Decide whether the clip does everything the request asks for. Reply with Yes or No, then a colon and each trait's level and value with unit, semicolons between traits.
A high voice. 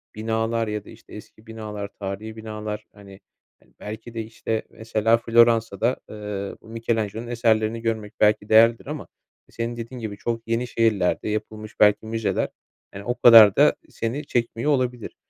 No: low, 110 Hz